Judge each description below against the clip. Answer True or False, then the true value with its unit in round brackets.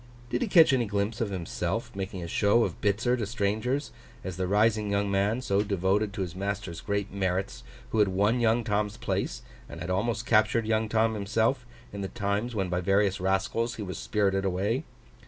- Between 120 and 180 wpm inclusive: False (195 wpm)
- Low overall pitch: True (100 Hz)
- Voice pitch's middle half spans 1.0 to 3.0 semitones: True (2.6 semitones)